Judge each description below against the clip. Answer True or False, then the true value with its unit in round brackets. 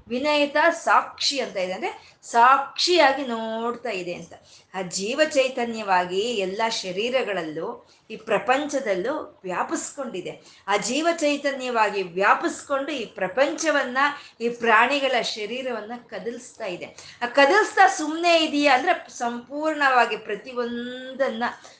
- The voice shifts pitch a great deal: False (4.7 semitones)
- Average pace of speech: True (95 wpm)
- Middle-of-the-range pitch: False (250 Hz)